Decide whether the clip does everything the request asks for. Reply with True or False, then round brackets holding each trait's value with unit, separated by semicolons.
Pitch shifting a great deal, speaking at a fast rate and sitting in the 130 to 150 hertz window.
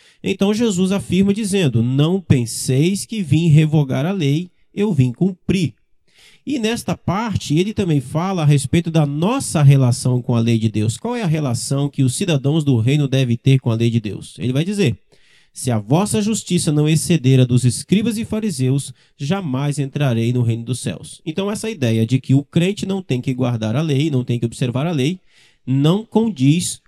True (6.3 semitones; 195 wpm; 145 Hz)